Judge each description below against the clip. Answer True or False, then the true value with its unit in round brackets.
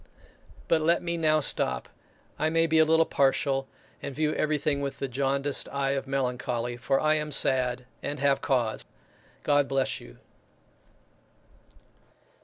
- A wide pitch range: False (2.6 semitones)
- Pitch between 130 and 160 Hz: True (140 Hz)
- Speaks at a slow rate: False (145 wpm)